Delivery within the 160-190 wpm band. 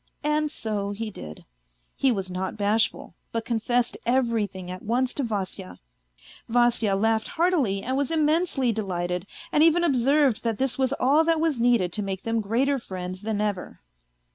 Yes: average, 165 wpm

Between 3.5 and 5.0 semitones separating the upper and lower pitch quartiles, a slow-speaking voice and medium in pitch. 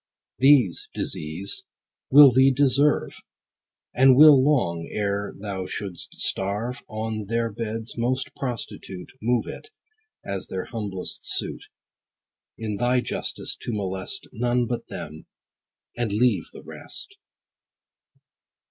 No: average, 4.1 semitones; slow, 110 wpm; low, 115 Hz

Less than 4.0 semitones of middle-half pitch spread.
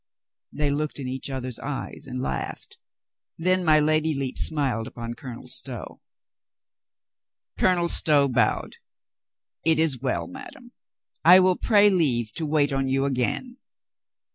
No: average, 4.3 semitones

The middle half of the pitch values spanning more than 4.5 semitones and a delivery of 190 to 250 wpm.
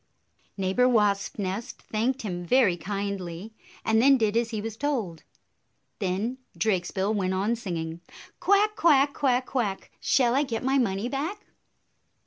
No: average, 5.2 semitones; average, 140 wpm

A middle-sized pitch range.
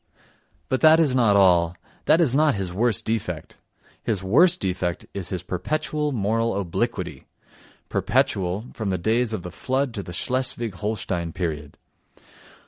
No: wide, 5.8 semitones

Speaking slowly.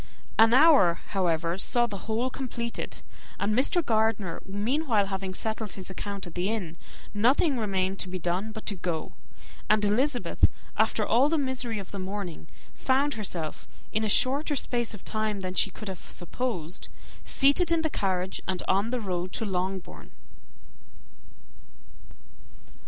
No: average, 150 wpm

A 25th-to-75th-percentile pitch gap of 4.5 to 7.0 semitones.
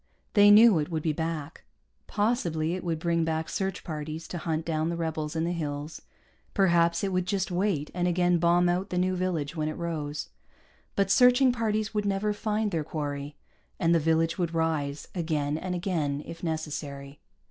No: average, 3.0 semitones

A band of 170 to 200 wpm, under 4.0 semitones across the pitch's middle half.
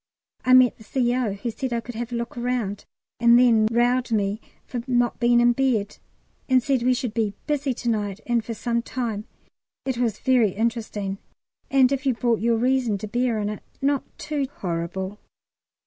Yes: average, 190 wpm; average, 2.8 semitones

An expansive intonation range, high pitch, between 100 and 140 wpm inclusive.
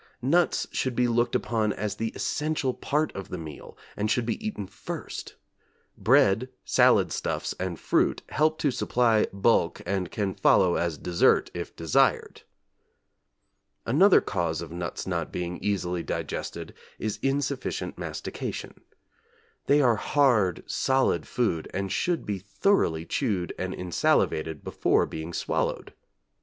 No: wide, 6.7 semitones; low, 105 Hz; slow, 135 wpm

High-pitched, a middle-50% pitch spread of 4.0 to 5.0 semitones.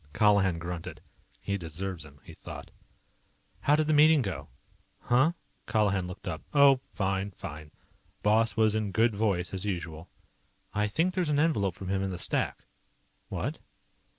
No: low, 100 Hz; average, 4.3 semitones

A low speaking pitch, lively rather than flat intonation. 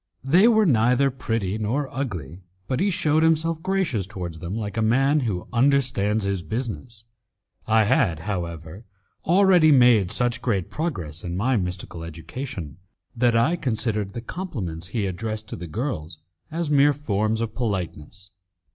Yes: low, 115 Hz; wide, 6.5 semitones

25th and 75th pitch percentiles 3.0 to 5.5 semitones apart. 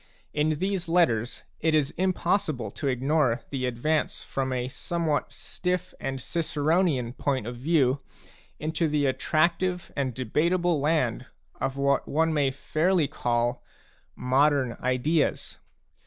Yes: average, 4.1 semitones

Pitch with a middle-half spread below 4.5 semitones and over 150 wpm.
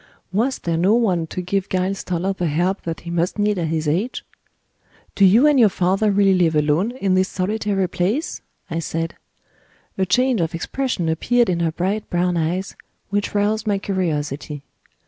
Yes: average, 3.5 semitones; average, 180 wpm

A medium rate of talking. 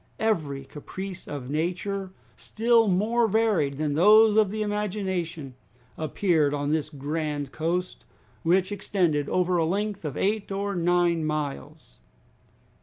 No: slow, 125 wpm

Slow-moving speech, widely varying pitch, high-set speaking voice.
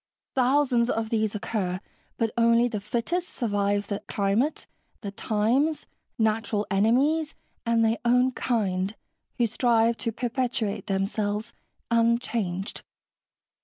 No: slow, 110 wpm; average, 2.9 semitones; high, 225 Hz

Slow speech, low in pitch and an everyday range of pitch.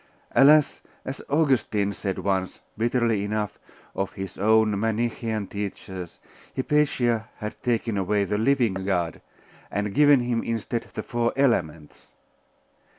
Yes: slow, 120 wpm; low, 110 Hz; average, 3.2 semitones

